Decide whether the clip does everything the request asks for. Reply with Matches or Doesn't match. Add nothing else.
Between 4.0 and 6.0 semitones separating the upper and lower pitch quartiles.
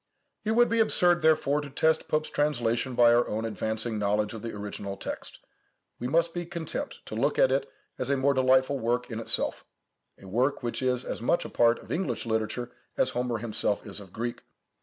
Matches